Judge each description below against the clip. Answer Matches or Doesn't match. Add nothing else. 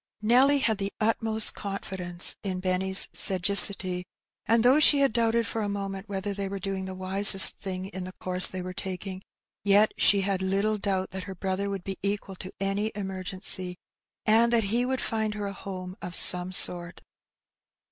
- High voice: Matches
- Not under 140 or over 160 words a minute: Doesn't match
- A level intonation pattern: Matches